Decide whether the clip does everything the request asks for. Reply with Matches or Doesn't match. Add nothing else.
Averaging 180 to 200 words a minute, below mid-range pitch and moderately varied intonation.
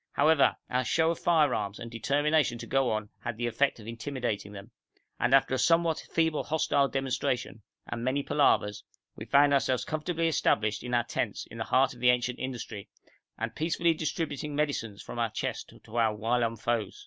Matches